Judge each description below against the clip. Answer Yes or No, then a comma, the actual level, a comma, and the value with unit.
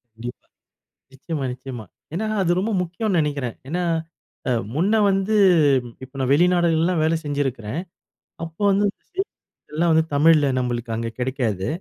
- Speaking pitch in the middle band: Yes, medium, 155 Hz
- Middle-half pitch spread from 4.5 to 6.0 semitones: Yes, wide, 5.6 semitones